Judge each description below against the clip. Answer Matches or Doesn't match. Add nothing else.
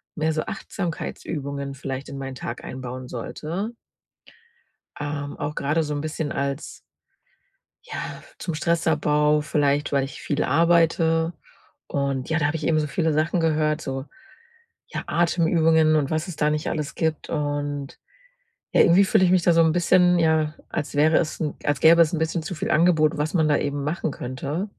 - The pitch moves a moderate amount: Doesn't match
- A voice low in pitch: Doesn't match